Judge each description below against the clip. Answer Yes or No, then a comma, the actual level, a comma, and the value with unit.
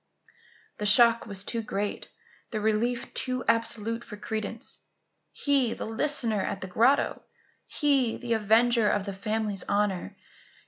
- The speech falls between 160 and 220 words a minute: No, slow, 135 wpm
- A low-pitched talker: No, high, 225 Hz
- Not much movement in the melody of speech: Yes, narrow, 2.3 semitones